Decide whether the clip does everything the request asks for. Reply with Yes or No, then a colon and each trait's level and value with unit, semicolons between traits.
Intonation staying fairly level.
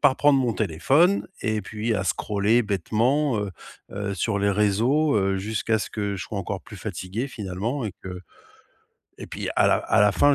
No: average, 3.4 semitones